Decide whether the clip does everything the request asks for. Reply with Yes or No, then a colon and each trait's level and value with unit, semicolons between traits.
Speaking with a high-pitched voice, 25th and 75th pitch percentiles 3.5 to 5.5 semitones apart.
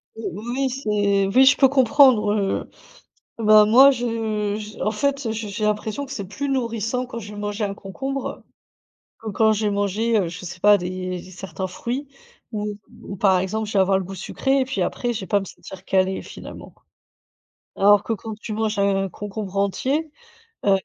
No: high, 210 Hz; average, 3.0 semitones